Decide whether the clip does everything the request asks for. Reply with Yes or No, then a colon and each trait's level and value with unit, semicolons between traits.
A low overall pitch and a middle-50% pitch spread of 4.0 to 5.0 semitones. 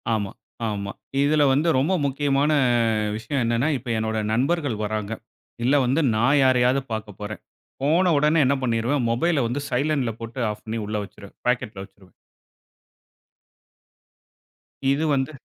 Yes: low, 125 Hz; average, 4.5 semitones